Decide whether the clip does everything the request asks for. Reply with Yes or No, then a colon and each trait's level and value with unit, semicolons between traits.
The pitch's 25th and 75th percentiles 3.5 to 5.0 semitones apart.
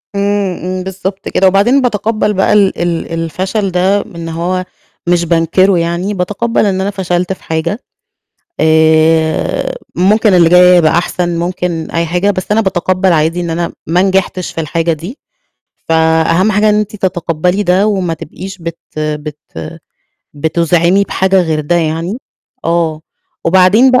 No: average, 2.7 semitones